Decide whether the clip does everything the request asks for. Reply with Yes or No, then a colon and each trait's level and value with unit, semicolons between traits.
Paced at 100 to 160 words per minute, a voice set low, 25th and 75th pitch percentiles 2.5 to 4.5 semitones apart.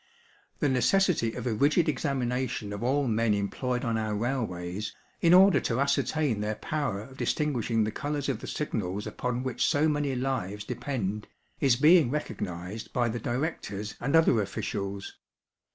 No: average, 155 wpm; low, 125 Hz; average, 5.1 semitones